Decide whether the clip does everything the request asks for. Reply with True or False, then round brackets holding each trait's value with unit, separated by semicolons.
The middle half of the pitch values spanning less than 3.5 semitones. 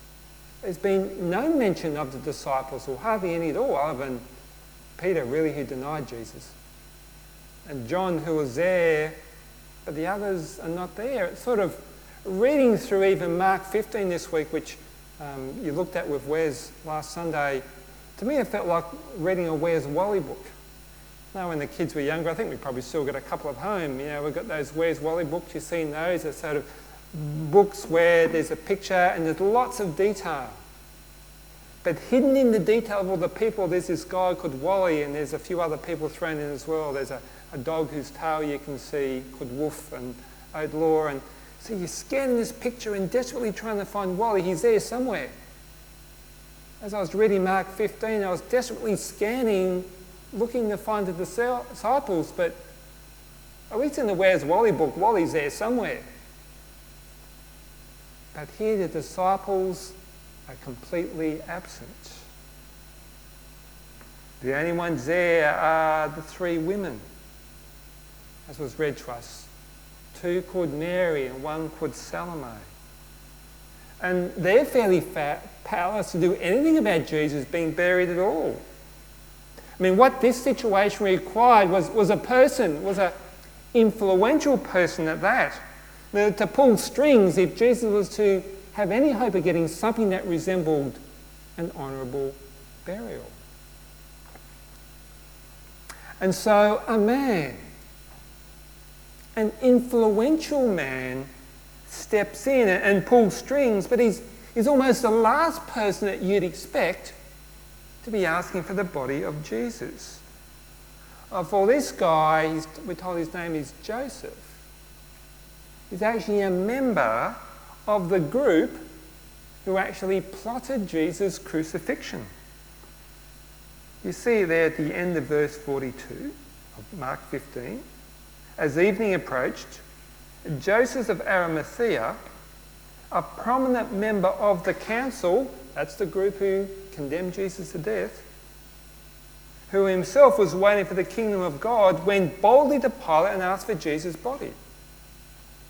False (5.1 semitones)